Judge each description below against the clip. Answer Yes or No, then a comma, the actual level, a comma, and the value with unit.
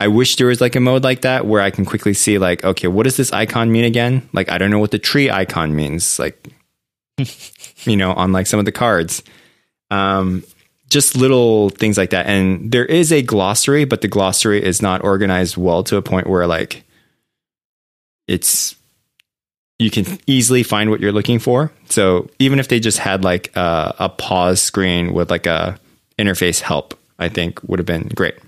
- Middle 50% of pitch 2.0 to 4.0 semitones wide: No, average, 4.8 semitones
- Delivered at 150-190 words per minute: No, average, 200 wpm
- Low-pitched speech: Yes, low, 105 Hz